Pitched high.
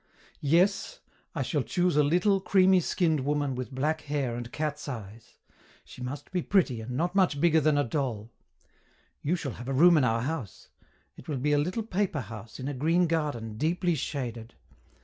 No: medium, 145 Hz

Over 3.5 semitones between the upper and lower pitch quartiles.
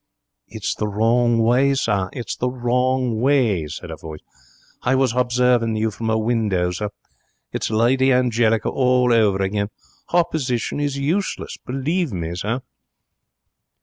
No: average, 3.1 semitones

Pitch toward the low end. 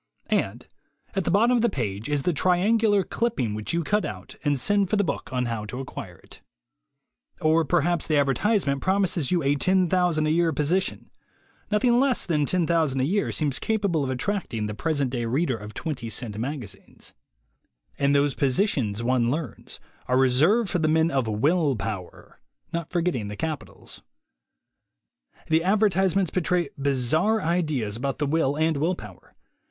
No: medium, 155 Hz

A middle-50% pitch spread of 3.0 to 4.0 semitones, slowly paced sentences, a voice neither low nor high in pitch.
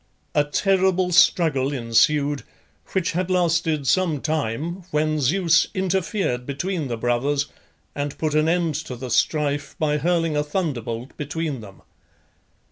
Yes: average, 3.7 semitones; slow, 130 wpm; medium, 150 Hz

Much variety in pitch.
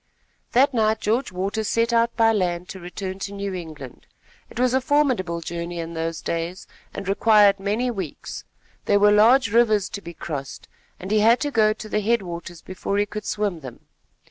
No: average, 4.3 semitones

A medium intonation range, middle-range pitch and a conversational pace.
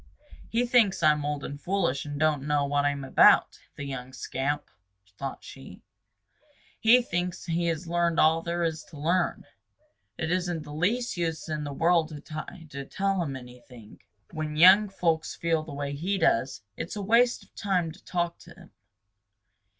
Yes: average, 3.6 semitones; medium, 160 Hz; average, 180 wpm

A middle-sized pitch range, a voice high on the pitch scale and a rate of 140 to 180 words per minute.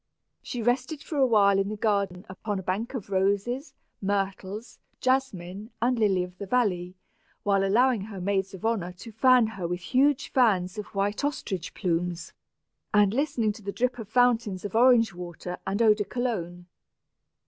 Yes: average, 4.3 semitones; high, 205 Hz; average, 175 wpm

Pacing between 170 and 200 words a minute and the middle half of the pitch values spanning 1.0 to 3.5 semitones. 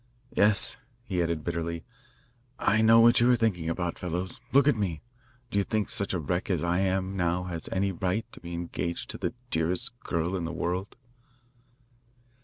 Yes: average, 185 wpm; average, 3.1 semitones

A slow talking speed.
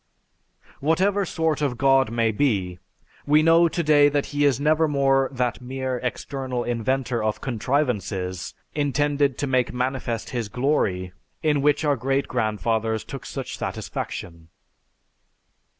Yes: slow, 125 wpm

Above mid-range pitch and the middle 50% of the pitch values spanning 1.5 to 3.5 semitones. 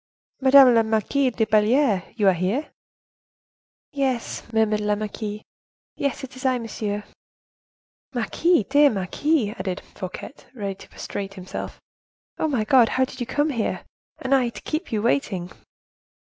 No: high, 230 Hz; average, 4.4 semitones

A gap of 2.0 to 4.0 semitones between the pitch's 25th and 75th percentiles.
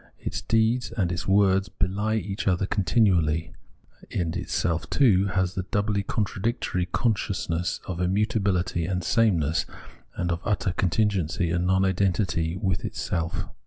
Yes: average, 2.7 semitones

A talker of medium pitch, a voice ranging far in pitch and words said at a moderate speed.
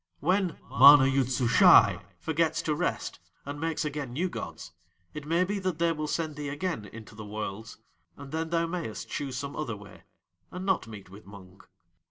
Yes: medium, 145 Hz; wide, 6.3 semitones; average, 185 wpm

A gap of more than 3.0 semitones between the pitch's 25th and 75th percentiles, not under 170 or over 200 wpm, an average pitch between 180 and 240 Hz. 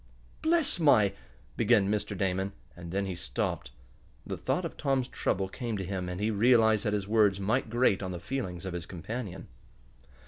No: average, 3.7 semitones; average, 185 wpm; low, 100 Hz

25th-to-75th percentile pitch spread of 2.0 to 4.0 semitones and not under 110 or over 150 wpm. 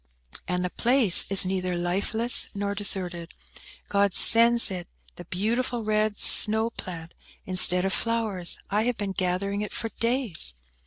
Yes: average, 3.7 semitones; average, 145 wpm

